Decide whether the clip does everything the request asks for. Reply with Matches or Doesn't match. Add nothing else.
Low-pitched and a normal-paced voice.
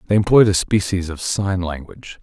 Matches